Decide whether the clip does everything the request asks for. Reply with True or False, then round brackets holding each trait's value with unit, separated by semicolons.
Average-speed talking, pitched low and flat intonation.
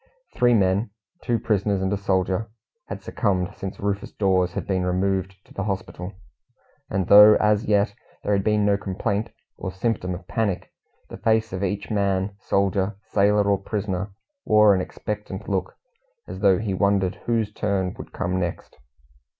True (165 wpm; 100 Hz; 1.8 semitones)